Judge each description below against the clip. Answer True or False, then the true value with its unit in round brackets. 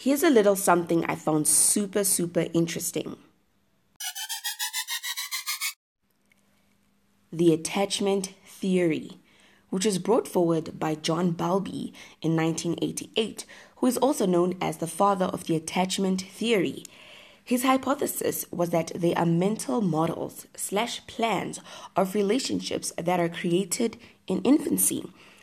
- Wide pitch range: False (4.3 semitones)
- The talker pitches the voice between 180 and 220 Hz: True (190 Hz)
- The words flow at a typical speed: False (115 wpm)